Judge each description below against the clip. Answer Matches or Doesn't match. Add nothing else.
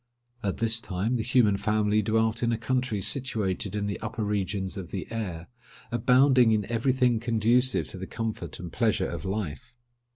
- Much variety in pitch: Doesn't match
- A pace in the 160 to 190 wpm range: Matches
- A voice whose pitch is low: Matches